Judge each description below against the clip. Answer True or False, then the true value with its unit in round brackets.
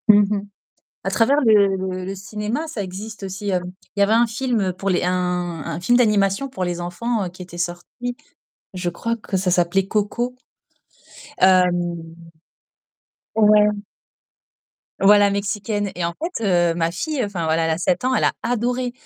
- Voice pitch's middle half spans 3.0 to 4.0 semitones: True (3.7 semitones)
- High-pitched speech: True (200 Hz)